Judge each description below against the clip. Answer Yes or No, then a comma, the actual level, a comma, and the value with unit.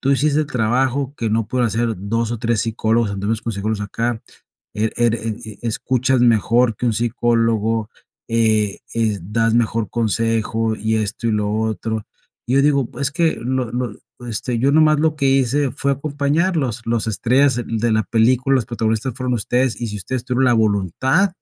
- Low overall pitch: Yes, low, 115 Hz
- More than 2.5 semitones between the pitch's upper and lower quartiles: Yes, average, 2.9 semitones